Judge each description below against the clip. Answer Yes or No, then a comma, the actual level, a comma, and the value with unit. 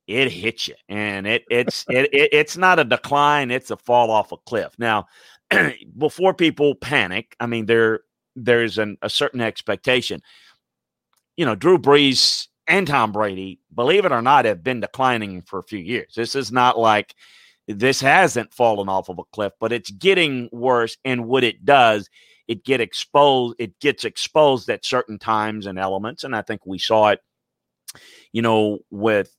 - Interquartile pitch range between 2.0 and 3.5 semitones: No, average, 4.1 semitones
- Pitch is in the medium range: No, low, 120 Hz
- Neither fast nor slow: Yes, average, 175 wpm